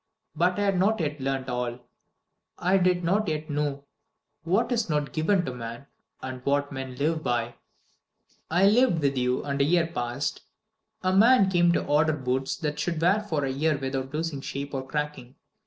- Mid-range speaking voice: Yes, medium, 150 Hz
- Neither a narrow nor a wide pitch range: Yes, average, 4.8 semitones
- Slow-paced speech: No, average, 185 wpm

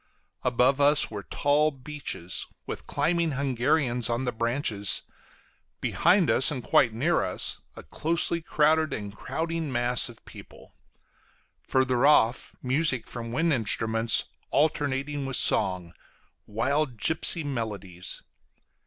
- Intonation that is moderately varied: Yes, average, 4.5 semitones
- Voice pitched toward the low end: Yes, low, 130 Hz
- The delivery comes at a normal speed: No, slow, 115 wpm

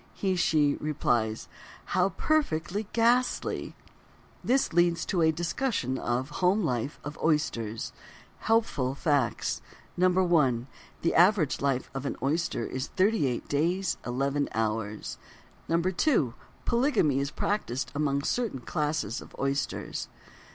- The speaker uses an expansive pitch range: Yes, wide, 6.0 semitones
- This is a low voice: No, medium, 150 Hz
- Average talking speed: No, slow, 115 wpm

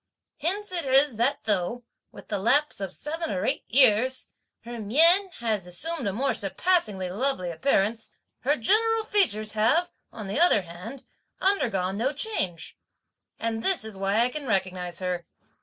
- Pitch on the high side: Yes, high, 230 Hz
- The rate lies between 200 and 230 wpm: No, average, 155 wpm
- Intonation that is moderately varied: No, wide, 7.4 semitones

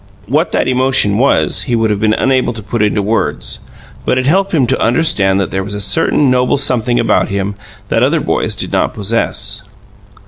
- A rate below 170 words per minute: No, average, 200 wpm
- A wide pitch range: No, average, 4.1 semitones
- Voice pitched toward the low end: Yes, low, 115 Hz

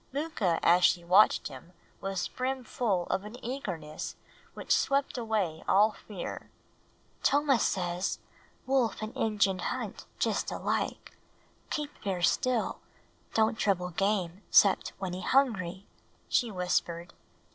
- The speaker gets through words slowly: Yes, slow, 125 wpm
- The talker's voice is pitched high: Yes, high, 200 Hz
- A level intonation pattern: No, average, 4.8 semitones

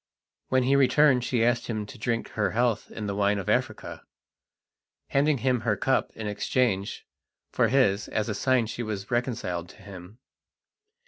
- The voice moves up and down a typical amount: Yes, average, 3.7 semitones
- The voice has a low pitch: Yes, low, 115 Hz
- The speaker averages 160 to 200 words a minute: Yes, average, 170 wpm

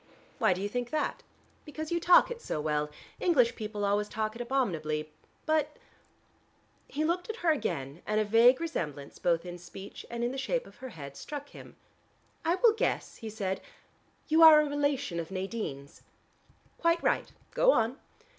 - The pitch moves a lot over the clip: Yes, wide, 8.8 semitones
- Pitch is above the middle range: Yes, high, 235 Hz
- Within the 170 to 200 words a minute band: Yes, average, 180 wpm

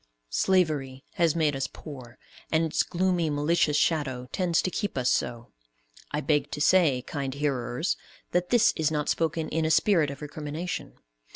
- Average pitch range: Yes, average, 3.4 semitones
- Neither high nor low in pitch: Yes, medium, 150 Hz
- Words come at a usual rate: Yes, average, 160 wpm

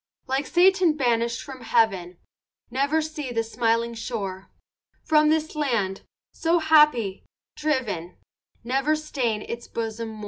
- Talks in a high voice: Yes, high, 245 Hz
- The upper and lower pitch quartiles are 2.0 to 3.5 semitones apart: No, average, 5.3 semitones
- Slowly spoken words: Yes, slow, 125 wpm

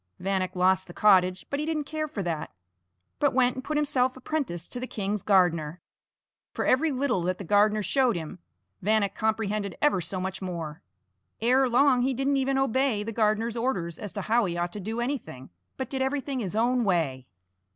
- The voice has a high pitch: Yes, high, 215 Hz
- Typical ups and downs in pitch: No, wide, 6.0 semitones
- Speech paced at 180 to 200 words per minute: Yes, average, 195 wpm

